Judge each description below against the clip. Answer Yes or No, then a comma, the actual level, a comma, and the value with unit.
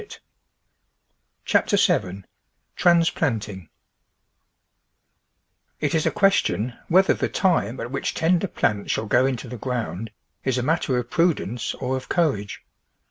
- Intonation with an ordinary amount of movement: No, wide, 6.7 semitones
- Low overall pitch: Yes, low, 130 Hz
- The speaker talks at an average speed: No, slow, 130 wpm